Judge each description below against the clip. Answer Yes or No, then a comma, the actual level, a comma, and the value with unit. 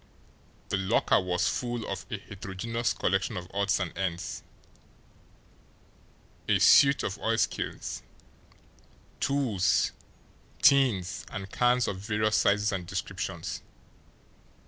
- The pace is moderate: No, slow, 100 wpm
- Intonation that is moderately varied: Yes, average, 3.9 semitones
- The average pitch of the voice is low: Yes, low, 100 Hz